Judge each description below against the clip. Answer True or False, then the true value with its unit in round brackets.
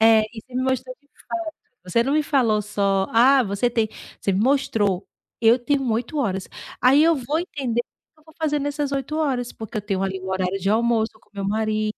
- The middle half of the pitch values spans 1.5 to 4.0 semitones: False (4.9 semitones)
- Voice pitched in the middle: False (235 Hz)